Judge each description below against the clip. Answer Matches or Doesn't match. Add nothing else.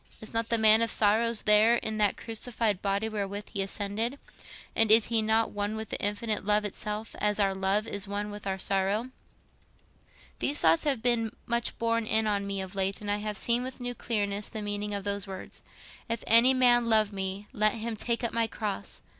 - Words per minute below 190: Doesn't match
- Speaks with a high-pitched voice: Matches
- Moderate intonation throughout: Doesn't match